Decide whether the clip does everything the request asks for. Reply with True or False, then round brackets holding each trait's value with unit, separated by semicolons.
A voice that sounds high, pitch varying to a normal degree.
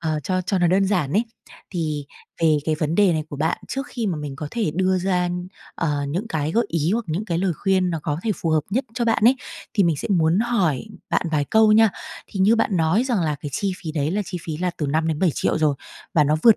False (175 Hz; 4.6 semitones)